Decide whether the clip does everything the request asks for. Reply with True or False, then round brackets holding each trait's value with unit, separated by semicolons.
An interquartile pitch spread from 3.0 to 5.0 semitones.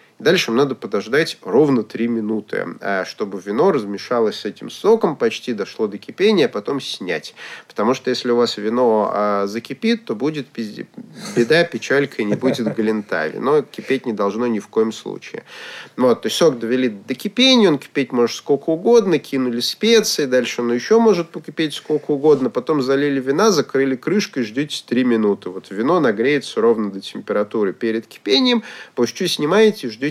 False (5.5 semitones)